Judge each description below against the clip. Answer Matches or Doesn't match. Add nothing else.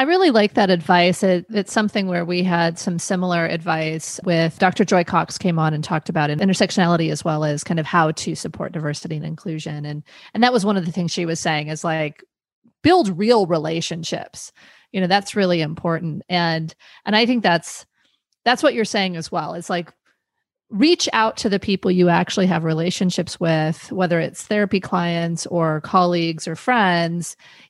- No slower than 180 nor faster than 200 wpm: Matches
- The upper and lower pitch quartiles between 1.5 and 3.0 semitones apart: Doesn't match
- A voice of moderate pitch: Matches